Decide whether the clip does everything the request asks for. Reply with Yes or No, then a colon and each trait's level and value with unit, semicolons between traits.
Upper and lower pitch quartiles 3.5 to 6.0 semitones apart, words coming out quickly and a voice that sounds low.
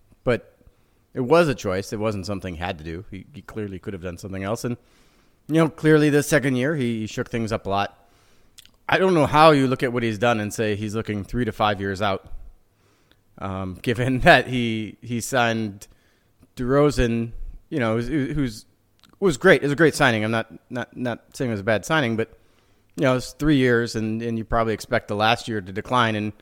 Yes: average, 4.0 semitones; fast, 225 wpm; low, 115 Hz